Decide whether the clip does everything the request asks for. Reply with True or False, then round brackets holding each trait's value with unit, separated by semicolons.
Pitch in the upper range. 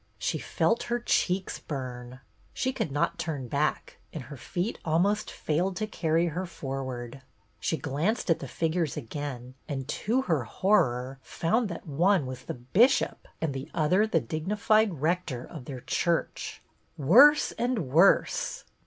False (160 Hz)